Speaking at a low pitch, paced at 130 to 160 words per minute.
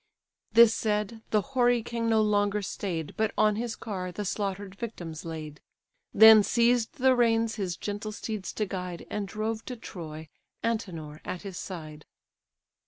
No: high, 210 Hz; average, 155 wpm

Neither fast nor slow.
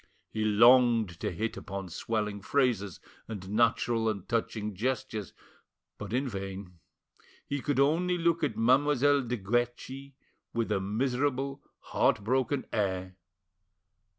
No: slow, 125 wpm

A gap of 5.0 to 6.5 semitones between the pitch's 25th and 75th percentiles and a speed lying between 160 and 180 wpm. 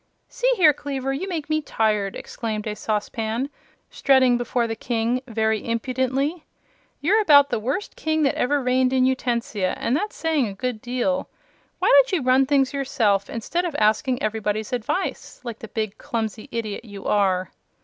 No: average, 4.4 semitones; average, 170 wpm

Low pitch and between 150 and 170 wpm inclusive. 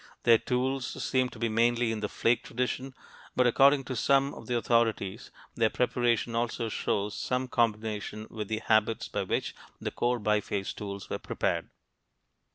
Yes: low, 115 Hz; average, 165 wpm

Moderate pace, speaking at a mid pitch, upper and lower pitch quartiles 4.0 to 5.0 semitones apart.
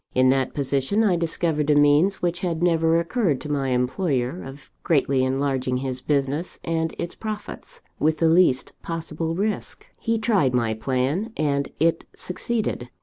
Yes: average, 155 wpm; medium, 155 Hz; average, 4.5 semitones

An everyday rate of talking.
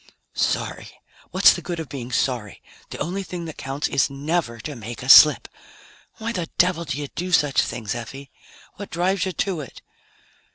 Yes: average, 180 wpm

